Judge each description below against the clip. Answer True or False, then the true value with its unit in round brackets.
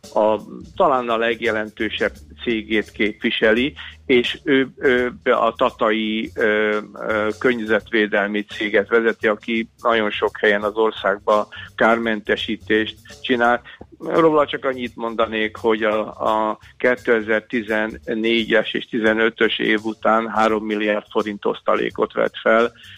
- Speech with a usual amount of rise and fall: False (1.4 semitones)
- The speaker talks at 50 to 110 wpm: True (105 wpm)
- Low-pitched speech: True (110 Hz)